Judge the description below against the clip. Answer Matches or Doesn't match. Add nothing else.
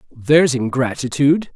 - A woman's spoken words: Doesn't match